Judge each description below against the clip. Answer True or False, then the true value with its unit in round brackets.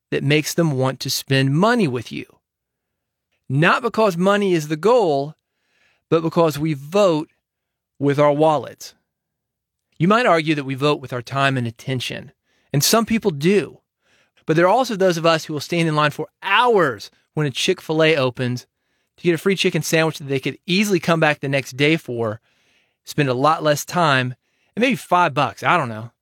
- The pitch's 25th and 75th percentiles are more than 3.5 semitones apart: True (4.4 semitones)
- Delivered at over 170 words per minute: True (195 wpm)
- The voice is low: False (155 Hz)